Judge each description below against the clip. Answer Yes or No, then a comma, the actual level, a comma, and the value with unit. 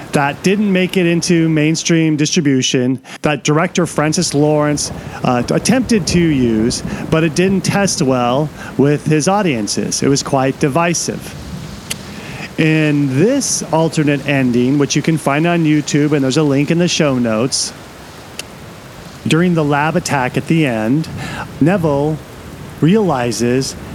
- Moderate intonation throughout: Yes, average, 3.4 semitones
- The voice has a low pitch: No, medium, 150 Hz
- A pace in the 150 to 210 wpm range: No, slow, 135 wpm